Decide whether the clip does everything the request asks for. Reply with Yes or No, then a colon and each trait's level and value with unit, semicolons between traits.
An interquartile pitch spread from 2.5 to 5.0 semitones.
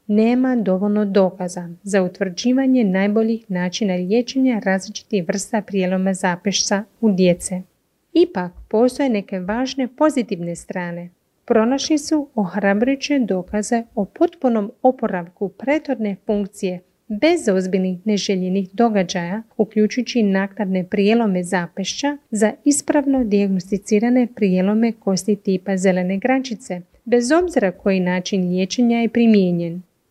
Yes: average, 4.2 semitones